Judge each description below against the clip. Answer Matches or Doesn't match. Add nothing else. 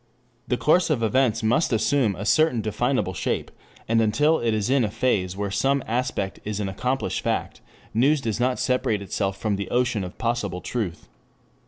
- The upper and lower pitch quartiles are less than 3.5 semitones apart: Doesn't match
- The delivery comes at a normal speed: Matches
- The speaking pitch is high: Doesn't match